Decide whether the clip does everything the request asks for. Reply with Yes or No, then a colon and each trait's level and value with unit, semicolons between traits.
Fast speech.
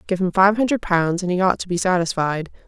Yes: fast, 245 wpm